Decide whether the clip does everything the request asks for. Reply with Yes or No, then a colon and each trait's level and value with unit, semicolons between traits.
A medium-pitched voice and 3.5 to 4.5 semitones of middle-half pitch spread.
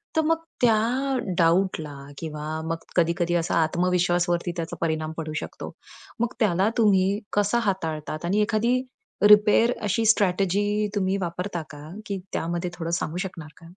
Yes: medium, 180 Hz; average, 3.8 semitones